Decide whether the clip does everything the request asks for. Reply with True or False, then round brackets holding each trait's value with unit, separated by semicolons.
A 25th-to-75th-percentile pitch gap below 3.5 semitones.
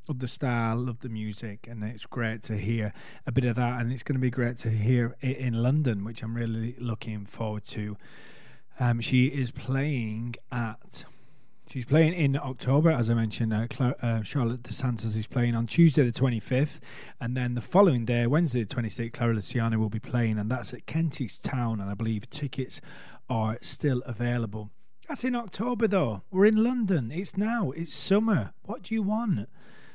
False (4.0 semitones)